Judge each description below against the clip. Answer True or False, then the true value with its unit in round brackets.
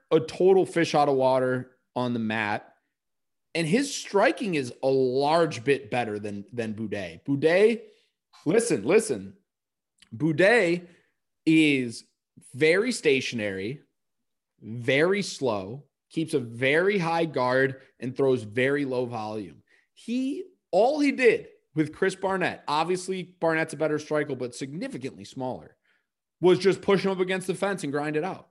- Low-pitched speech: False (150 Hz)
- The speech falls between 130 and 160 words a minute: True (140 wpm)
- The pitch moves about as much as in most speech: False (6.7 semitones)